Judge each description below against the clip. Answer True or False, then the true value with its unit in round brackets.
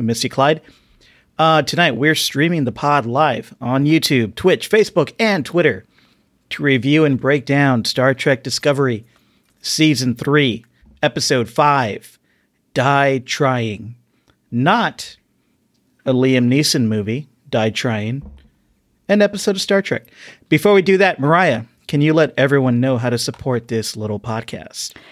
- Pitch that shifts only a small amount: False (4.3 semitones)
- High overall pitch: False (140 Hz)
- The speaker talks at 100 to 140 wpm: True (135 wpm)